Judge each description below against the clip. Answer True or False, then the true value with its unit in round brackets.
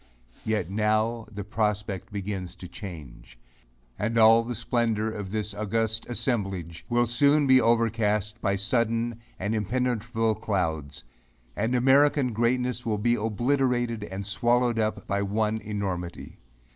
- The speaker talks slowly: True (125 wpm)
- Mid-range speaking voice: False (110 Hz)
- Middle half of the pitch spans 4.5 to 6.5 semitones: False (2.9 semitones)